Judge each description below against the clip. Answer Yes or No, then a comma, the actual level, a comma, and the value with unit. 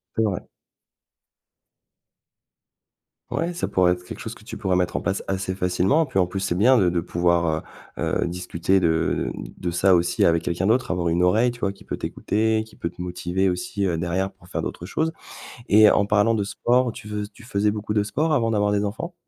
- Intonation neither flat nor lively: Yes, average, 3.5 semitones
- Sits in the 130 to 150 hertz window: No, very low, 95 Hz